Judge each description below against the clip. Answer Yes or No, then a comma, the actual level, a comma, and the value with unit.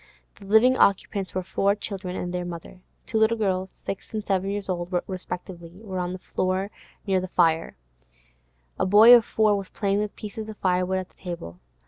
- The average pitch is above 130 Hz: Yes, high, 190 Hz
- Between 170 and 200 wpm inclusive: Yes, average, 190 wpm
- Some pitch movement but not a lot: No, narrow, 2.3 semitones